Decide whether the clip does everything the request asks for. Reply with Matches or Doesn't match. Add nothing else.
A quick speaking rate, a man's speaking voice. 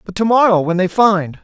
Matches